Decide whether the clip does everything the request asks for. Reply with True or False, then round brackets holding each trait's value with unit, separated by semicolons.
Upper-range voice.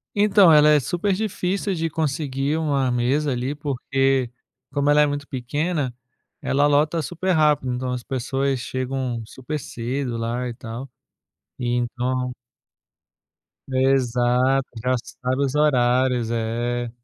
False (135 Hz)